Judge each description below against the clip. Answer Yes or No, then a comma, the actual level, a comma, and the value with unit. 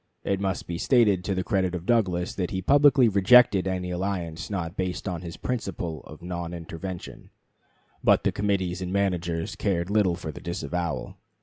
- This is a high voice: No, very low, 90 Hz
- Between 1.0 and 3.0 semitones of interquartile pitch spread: Yes, narrow, 2.5 semitones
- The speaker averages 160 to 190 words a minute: Yes, average, 175 wpm